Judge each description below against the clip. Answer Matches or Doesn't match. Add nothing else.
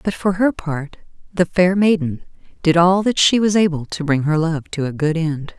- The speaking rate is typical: Doesn't match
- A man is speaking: Doesn't match